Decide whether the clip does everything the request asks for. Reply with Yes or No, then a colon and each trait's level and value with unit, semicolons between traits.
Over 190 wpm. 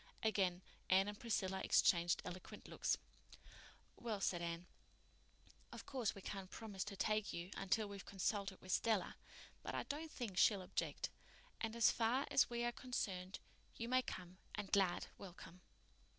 No: average, 155 wpm